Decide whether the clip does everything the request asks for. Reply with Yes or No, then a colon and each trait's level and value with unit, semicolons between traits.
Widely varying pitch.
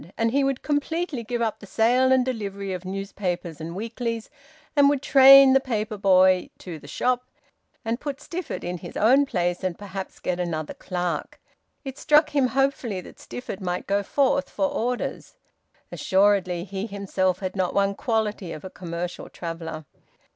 Yes: wide, 6.0 semitones